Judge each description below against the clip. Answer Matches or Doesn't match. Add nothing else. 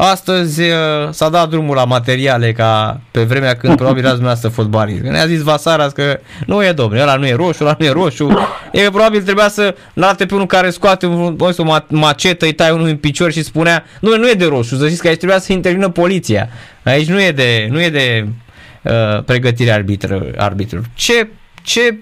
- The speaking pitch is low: Doesn't match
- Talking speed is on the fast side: Matches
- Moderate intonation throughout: Doesn't match